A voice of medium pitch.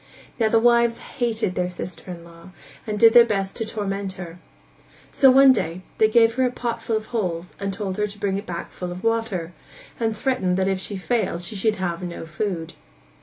No: high, 200 Hz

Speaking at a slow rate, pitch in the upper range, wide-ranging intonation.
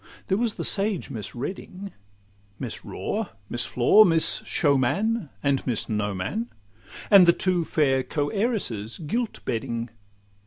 No: slow, 125 wpm; medium, 150 Hz; wide, 8.6 semitones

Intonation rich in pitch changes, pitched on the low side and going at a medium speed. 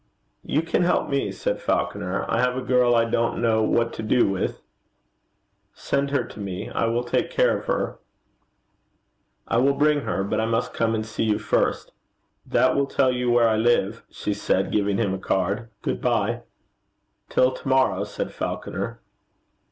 No: average, 2.9 semitones; low, 115 Hz; average, 180 wpm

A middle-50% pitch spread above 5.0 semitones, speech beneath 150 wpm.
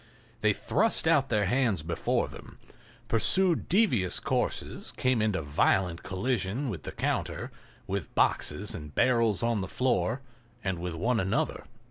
Yes: wide, 5.5 semitones; average, 140 wpm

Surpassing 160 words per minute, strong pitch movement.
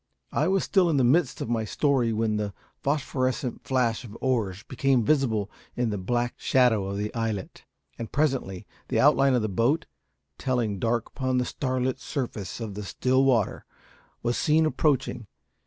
No: average, 170 wpm; average, 3.5 semitones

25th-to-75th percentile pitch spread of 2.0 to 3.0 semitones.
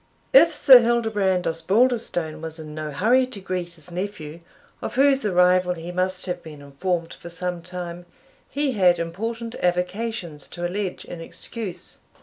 No: average, 4.6 semitones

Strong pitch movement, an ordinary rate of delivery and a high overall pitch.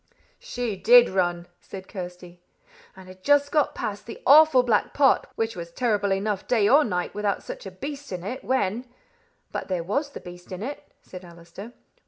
Yes: wide, 5.9 semitones; average, 190 wpm; high, 205 Hz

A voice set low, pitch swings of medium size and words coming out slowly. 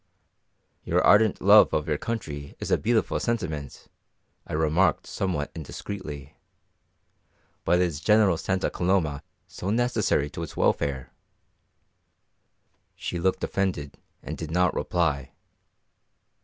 Yes: very low, 85 Hz; average, 5.0 semitones; slow, 115 wpm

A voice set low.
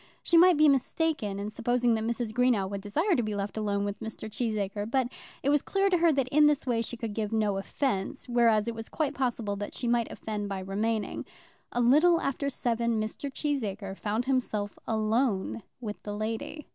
No: high, 230 Hz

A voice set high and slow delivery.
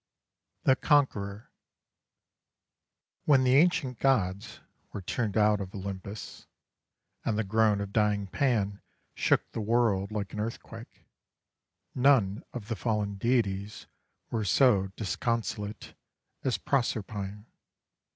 No: low, 105 Hz; slow, 110 wpm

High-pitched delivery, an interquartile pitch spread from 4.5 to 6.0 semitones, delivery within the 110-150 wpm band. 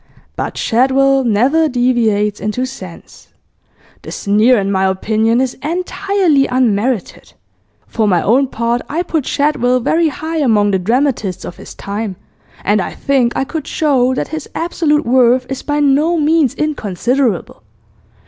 Yes: very high, 255 Hz; average, 5.2 semitones; average, 145 wpm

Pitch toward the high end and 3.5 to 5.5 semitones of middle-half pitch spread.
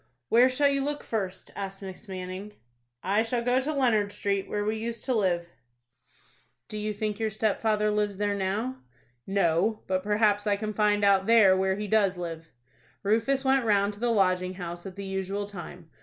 No: high, 205 Hz; narrow, 2.5 semitones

